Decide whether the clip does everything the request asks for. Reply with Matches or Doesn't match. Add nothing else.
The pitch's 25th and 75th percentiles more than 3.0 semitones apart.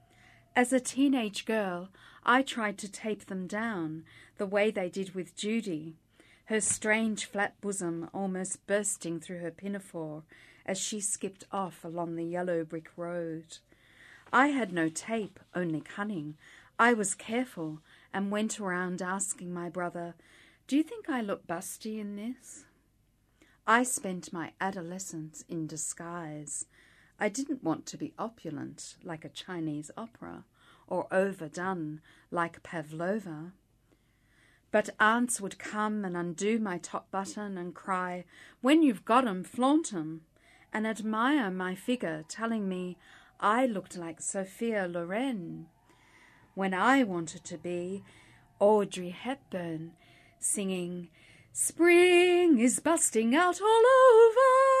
Matches